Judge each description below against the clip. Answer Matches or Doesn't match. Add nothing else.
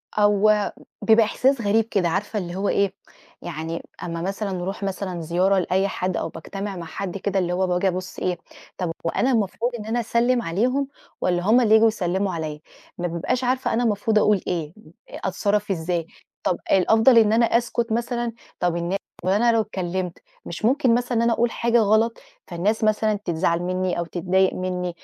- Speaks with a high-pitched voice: Matches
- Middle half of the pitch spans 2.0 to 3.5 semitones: Doesn't match